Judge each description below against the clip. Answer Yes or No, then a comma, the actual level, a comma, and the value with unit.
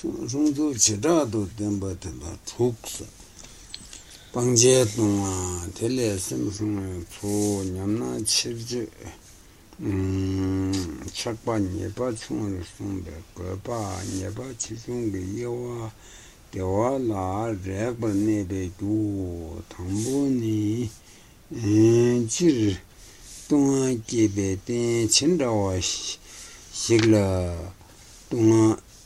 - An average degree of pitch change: Yes, average, 3.6 semitones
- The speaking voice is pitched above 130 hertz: No, low, 105 Hz